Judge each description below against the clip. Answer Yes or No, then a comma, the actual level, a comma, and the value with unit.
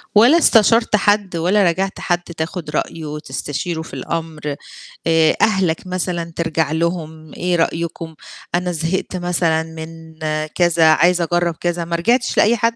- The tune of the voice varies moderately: No, narrow, 2.2 semitones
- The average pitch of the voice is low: No, medium, 170 Hz